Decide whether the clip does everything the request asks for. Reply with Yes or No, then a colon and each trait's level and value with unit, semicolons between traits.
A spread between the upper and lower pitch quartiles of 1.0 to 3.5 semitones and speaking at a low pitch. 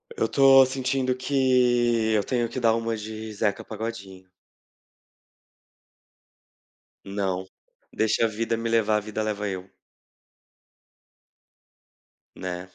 Yes: average, 2.9 semitones; low, 110 Hz